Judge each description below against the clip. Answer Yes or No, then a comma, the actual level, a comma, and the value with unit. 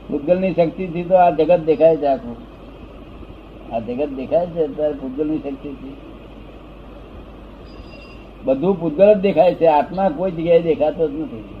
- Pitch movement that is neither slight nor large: Yes, average, 3.9 semitones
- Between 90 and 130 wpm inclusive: No, fast, 140 wpm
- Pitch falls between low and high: Yes, medium, 160 Hz